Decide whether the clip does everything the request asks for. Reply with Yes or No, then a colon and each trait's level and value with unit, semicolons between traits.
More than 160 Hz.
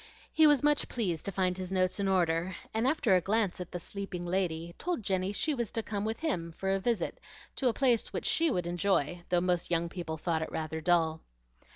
Yes: medium, 185 Hz